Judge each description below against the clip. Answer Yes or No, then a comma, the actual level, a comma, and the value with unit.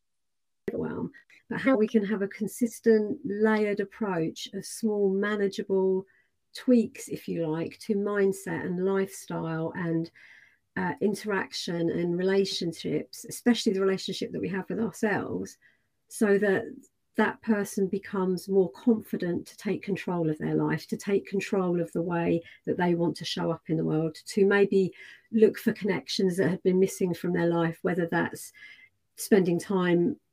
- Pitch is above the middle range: Yes, high, 195 Hz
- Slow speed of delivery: No, average, 155 wpm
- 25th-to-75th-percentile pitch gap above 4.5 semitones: No, average, 3.2 semitones